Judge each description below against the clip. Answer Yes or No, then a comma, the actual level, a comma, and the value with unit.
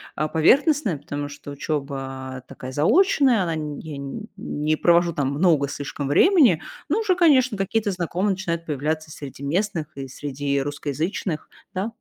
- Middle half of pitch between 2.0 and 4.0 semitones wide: No, wide, 5.5 semitones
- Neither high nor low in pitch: Yes, medium, 155 Hz